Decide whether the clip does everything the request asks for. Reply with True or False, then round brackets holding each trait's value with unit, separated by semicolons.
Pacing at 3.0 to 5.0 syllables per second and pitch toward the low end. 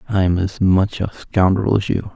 True (4.5 syllables/s; 95 Hz)